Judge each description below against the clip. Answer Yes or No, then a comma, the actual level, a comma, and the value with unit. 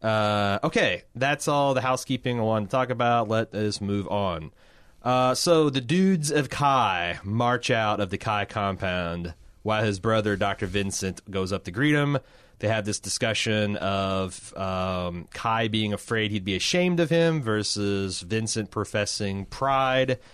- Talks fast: No, average, 160 wpm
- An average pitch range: Yes, average, 4.5 semitones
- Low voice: Yes, low, 105 Hz